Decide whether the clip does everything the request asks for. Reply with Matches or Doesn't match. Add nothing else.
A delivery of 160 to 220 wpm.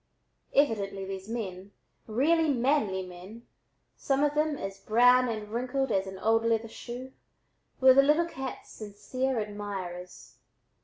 Doesn't match